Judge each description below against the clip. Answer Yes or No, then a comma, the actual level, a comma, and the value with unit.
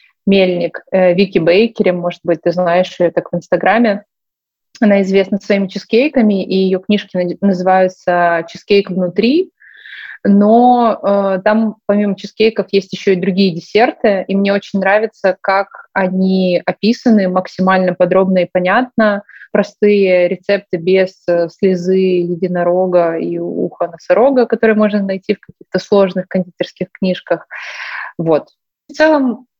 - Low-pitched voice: No, high, 190 Hz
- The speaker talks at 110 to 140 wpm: Yes, average, 125 wpm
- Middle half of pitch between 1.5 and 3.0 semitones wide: Yes, narrow, 2.4 semitones